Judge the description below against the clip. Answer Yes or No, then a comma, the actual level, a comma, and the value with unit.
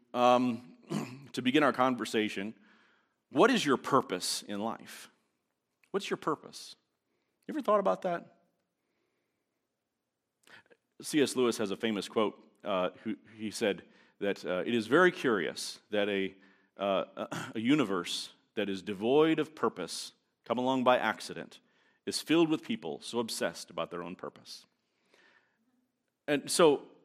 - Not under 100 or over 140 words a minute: Yes, slow, 135 wpm